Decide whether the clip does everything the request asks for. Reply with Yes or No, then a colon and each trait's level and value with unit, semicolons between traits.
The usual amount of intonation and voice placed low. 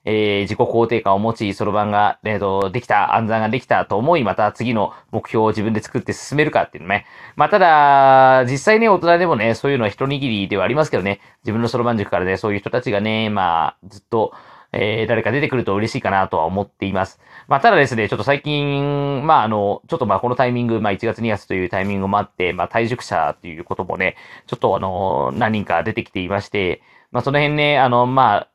Yes: average, 4.5 semitones; low, 110 Hz